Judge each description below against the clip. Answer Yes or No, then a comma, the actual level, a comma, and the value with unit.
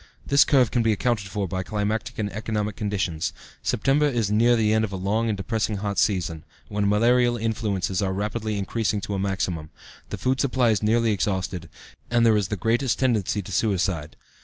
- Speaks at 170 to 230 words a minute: Yes, average, 190 wpm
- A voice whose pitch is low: Yes, low, 105 Hz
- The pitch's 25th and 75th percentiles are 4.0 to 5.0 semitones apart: No, average, 2.8 semitones